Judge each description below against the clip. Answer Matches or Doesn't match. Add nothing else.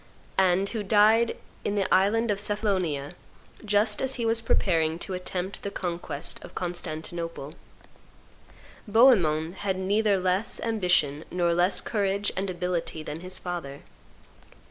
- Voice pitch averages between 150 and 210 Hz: Matches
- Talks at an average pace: Doesn't match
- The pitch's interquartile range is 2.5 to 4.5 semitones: Matches